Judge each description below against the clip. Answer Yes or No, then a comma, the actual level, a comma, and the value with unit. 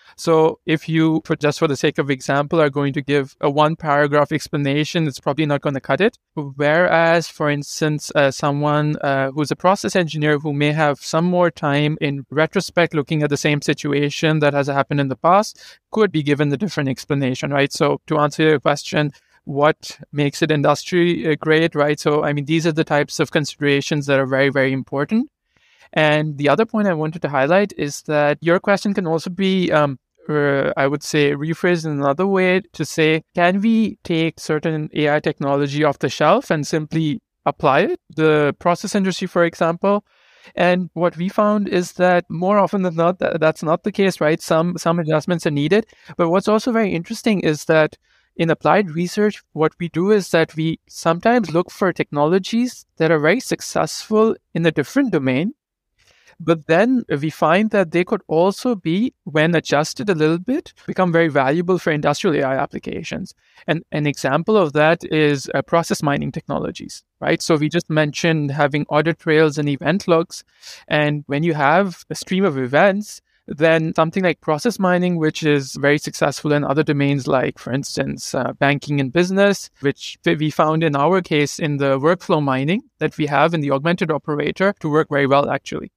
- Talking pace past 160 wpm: Yes, average, 190 wpm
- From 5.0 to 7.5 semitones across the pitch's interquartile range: No, average, 3.2 semitones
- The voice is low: No, medium, 160 Hz